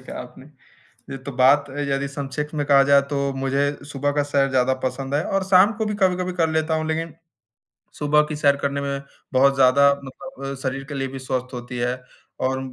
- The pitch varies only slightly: Yes, narrow, 2.0 semitones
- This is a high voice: No, medium, 140 Hz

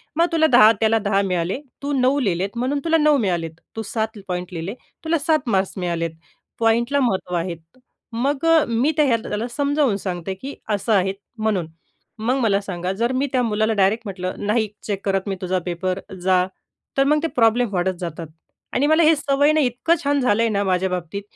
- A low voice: No, high, 220 Hz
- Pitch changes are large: Yes, wide, 6.1 semitones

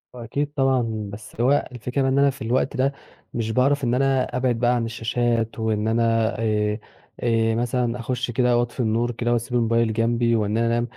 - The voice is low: Yes, low, 120 Hz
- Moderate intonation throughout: No, narrow, 1.8 semitones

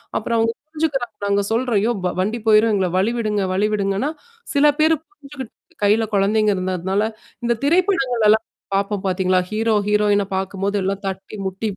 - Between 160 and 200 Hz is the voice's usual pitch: No, high, 210 Hz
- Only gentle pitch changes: No, average, 3.3 semitones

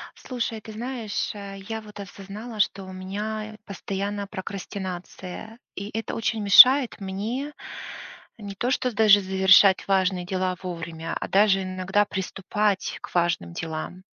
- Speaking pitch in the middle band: No, high, 200 Hz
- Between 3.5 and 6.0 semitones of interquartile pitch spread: No, narrow, 2.5 semitones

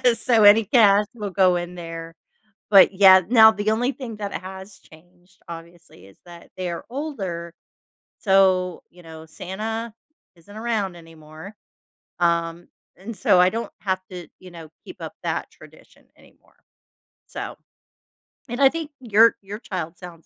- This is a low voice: No, high, 190 Hz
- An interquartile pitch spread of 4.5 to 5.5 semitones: No, average, 4.1 semitones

